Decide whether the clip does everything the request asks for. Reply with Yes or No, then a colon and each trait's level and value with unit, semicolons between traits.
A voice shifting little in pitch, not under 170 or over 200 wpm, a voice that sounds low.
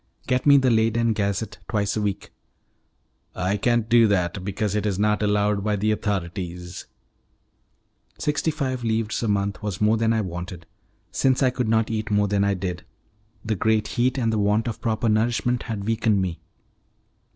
Yes: narrow, 2.3 semitones; average, 175 wpm; low, 105 Hz